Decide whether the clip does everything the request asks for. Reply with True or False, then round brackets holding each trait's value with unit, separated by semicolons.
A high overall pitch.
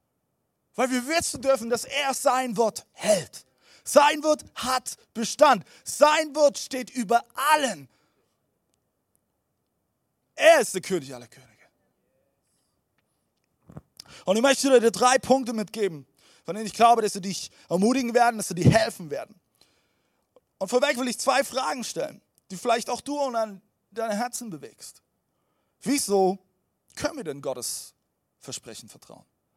True (240 Hz)